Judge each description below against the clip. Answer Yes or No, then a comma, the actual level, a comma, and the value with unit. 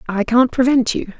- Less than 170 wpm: No, average, 200 wpm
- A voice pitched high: Yes, high, 240 Hz